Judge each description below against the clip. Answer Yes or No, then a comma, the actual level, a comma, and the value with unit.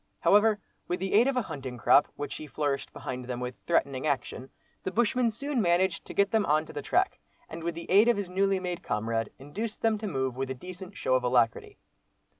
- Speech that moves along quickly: Yes, fast, 225 wpm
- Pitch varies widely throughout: Yes, wide, 7.5 semitones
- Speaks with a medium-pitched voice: Yes, medium, 170 Hz